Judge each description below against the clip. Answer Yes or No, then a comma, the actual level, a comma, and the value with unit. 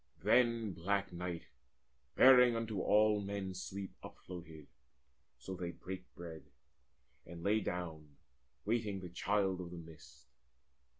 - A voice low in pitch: Yes, very low, 95 Hz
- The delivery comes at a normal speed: No, slow, 120 wpm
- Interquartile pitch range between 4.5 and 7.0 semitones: No, average, 3.3 semitones